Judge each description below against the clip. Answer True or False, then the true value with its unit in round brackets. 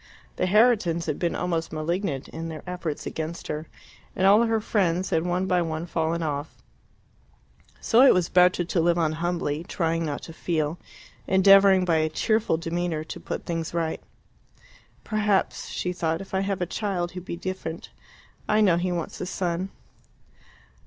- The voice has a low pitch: False (175 Hz)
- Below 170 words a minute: False (175 wpm)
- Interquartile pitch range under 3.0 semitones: True (2.6 semitones)